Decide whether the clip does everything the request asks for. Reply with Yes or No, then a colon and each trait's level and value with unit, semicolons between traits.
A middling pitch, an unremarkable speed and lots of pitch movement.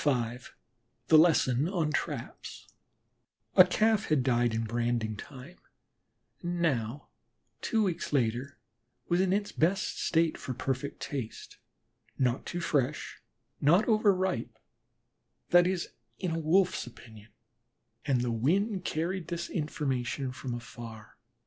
No: medium, 150 Hz; slow, 125 wpm; wide, 6.4 semitones